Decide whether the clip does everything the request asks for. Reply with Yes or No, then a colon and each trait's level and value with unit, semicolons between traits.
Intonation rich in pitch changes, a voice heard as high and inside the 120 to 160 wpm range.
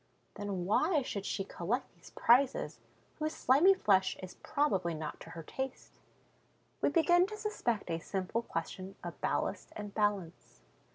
Yes: wide, 7.8 semitones; high, 210 Hz; average, 150 wpm